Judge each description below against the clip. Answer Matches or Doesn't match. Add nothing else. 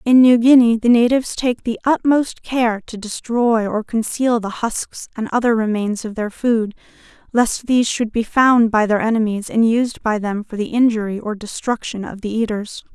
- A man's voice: Doesn't match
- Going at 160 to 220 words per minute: Matches